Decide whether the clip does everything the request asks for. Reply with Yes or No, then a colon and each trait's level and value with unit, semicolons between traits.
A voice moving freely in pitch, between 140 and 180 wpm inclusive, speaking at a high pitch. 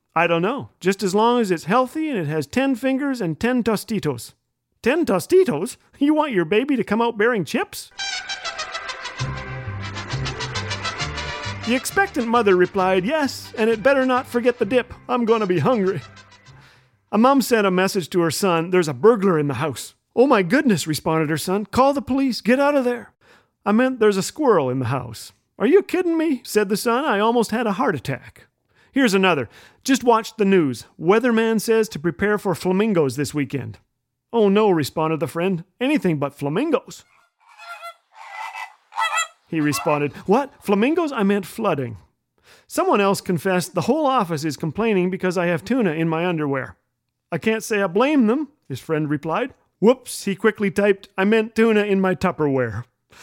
Yes: wide, 7.3 semitones; average, 175 wpm; high, 200 Hz